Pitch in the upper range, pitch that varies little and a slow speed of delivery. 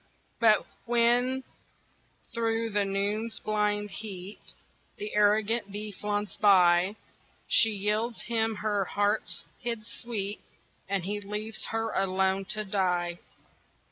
Yes: high, 210 Hz; narrow, 2.2 semitones; slow, 110 wpm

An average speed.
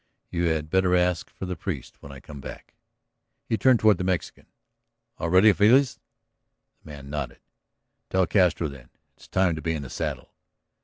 Yes: average, 175 wpm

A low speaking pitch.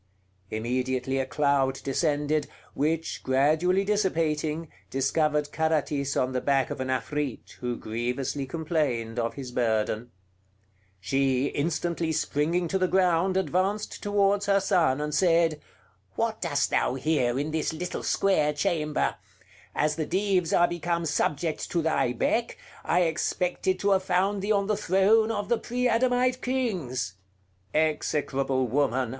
No: medium, 155 Hz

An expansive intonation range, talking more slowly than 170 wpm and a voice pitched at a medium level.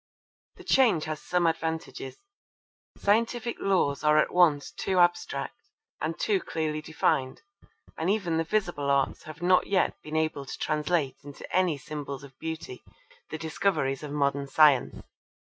No: average, 3.7 semitones; average, 145 wpm; medium, 160 Hz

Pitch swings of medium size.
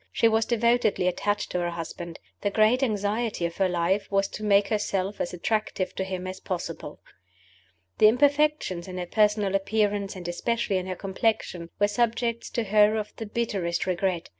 Yes: average, 3.2 semitones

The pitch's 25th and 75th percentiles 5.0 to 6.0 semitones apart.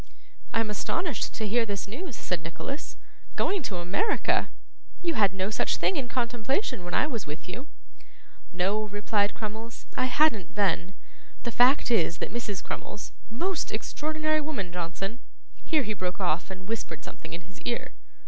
Yes: wide, 5.6 semitones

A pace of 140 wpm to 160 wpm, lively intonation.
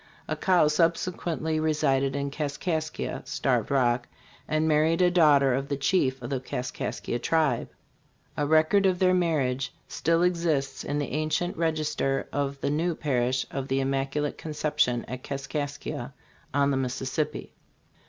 No: average, 145 wpm; average, 2.8 semitones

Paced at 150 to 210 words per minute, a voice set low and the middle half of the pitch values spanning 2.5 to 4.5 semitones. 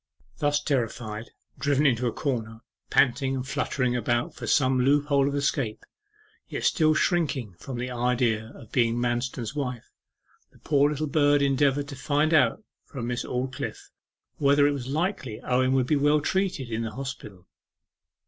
Yes: average, 160 wpm; low, 130 Hz; average, 3.1 semitones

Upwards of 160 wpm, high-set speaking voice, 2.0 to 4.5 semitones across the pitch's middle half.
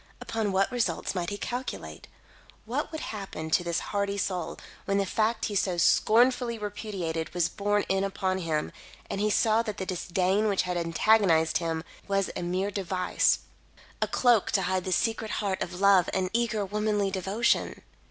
Yes: average, 170 wpm; high, 195 Hz; average, 2.7 semitones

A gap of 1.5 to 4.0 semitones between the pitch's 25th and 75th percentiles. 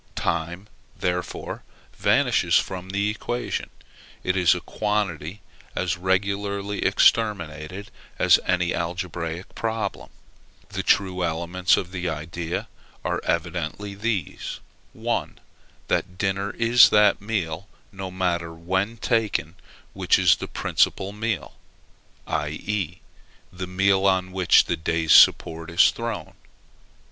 Yes: average, 3.0 semitones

